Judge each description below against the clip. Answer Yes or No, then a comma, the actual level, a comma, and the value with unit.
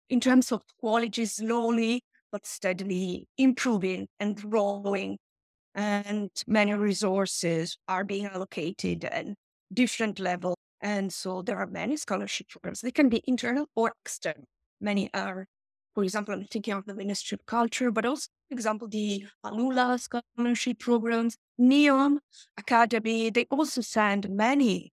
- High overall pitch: Yes, high, 220 Hz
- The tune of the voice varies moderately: Yes, average, 3.3 semitones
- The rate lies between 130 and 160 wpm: Yes, slow, 135 wpm